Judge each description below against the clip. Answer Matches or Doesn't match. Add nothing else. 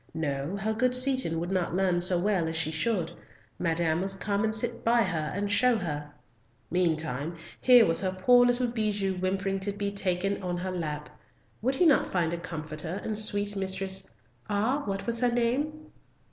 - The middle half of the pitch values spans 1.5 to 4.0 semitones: Doesn't match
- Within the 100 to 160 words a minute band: Doesn't match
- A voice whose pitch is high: Matches